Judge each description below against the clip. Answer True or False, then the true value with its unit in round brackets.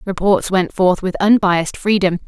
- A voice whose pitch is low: False (190 Hz)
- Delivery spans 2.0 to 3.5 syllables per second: False (4.8 syllables/s)